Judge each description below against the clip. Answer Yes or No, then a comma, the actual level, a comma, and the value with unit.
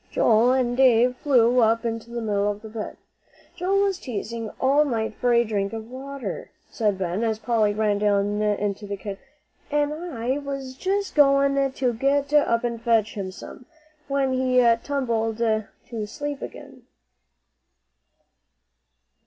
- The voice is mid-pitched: No, high, 235 Hz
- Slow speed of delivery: No, average, 150 wpm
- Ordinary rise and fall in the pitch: Yes, average, 4.1 semitones